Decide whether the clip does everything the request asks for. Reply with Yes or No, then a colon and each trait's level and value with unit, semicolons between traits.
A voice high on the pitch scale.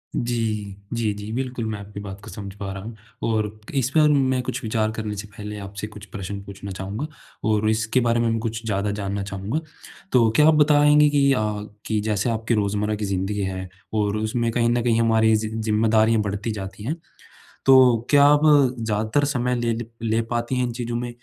No: low, 110 Hz